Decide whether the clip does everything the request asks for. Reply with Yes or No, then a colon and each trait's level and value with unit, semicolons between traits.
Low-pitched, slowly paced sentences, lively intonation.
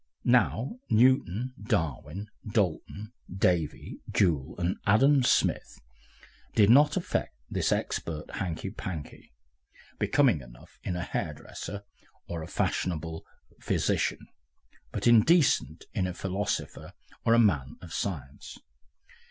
Yes: very low, 95 Hz; slow, 110 wpm; wide, 6.3 semitones